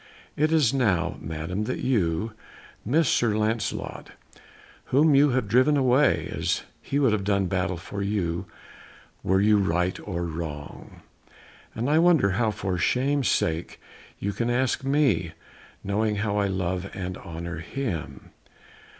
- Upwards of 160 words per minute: No, average, 140 wpm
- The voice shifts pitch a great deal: Yes, wide, 6.2 semitones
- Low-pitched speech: Yes, low, 105 Hz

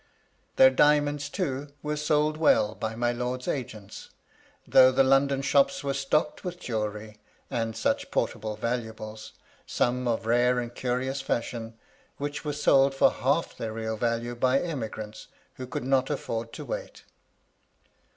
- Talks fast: No, average, 145 wpm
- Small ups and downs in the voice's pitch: No, average, 3.6 semitones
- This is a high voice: No, low, 125 Hz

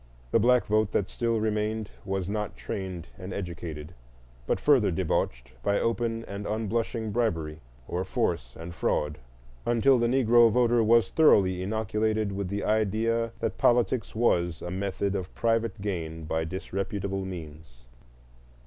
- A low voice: Yes, low, 100 Hz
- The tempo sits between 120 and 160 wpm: Yes, average, 140 wpm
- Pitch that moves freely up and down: No, average, 4.2 semitones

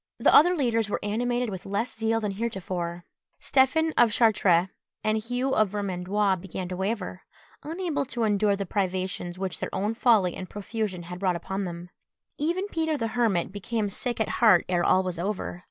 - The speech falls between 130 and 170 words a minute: No, average, 180 wpm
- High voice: Yes, high, 205 Hz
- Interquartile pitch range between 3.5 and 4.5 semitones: Yes, average, 4.1 semitones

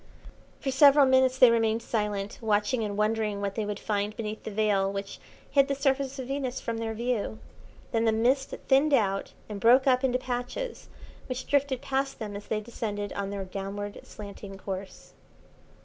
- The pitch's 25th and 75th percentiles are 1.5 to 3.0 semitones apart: No, average, 4.2 semitones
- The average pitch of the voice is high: Yes, high, 225 Hz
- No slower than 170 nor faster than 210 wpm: Yes, average, 180 wpm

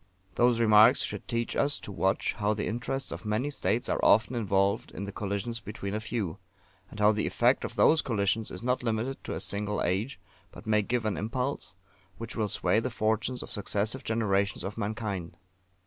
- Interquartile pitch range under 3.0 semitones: Yes, narrow, 2.6 semitones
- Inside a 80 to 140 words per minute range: No, average, 195 wpm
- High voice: No, low, 110 Hz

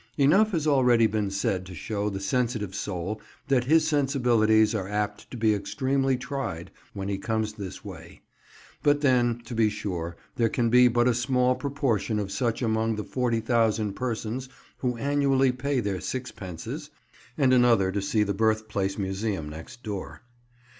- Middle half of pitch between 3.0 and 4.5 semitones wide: Yes, average, 3.9 semitones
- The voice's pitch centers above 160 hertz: No, low, 115 Hz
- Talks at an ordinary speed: Yes, average, 160 wpm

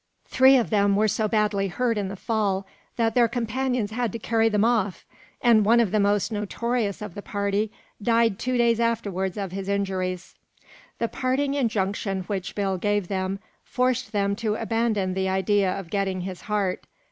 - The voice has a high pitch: Yes, high, 210 Hz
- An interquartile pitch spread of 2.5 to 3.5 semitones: Yes, average, 2.9 semitones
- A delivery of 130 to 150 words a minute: No, average, 180 wpm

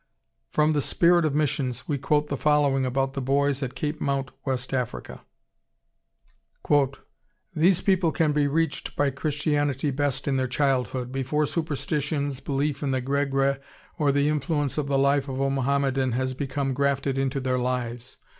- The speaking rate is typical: Yes, average, 165 wpm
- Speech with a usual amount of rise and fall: No, narrow, 1.8 semitones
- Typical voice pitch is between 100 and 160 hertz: Yes, medium, 140 Hz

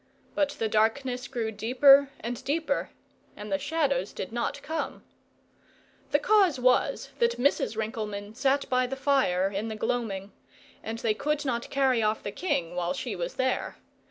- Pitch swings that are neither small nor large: Yes, average, 4.6 semitones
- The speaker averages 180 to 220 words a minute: No, average, 160 wpm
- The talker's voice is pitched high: Yes, high, 245 Hz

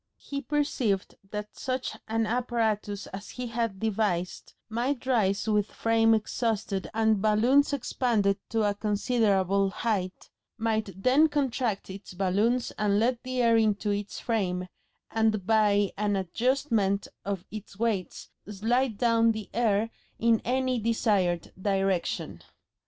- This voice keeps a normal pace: No, slow, 130 wpm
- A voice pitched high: Yes, high, 220 Hz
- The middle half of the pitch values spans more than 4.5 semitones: No, average, 2.8 semitones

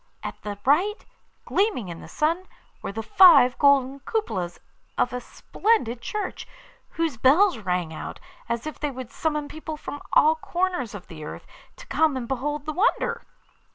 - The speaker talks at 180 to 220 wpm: No, average, 165 wpm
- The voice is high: Yes, very high, 290 Hz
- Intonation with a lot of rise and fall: Yes, wide, 6.0 semitones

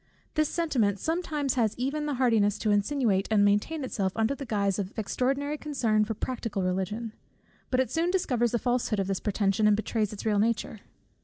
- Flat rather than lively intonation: No, average, 4.8 semitones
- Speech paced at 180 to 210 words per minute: Yes, average, 185 wpm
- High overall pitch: Yes, high, 225 Hz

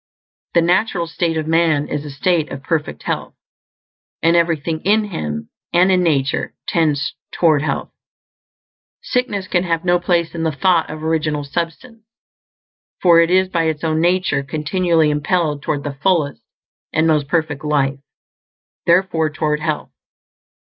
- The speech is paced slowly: No, average, 145 wpm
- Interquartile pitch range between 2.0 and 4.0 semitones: Yes, average, 2.8 semitones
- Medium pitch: Yes, medium, 160 Hz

